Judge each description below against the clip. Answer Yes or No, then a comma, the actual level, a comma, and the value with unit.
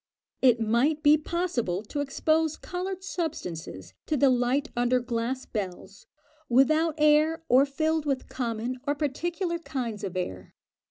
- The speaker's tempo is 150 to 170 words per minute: No, average, 140 wpm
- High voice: Yes, very high, 270 Hz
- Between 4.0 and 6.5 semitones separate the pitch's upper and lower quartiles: Yes, average, 5.1 semitones